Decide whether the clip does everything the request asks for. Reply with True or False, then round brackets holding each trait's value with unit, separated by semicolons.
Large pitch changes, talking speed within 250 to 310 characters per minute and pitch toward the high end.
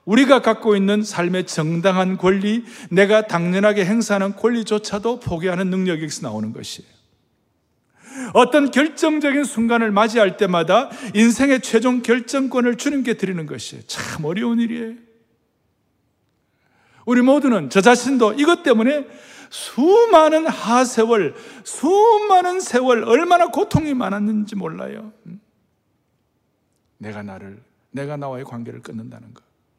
True (5.8 semitones; 280 characters per minute; 225 Hz)